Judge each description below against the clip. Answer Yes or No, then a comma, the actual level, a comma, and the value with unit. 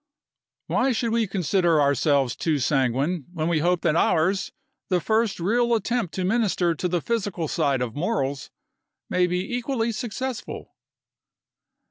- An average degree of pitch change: No, wide, 6.5 semitones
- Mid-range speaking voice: Yes, medium, 180 Hz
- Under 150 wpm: Yes, average, 140 wpm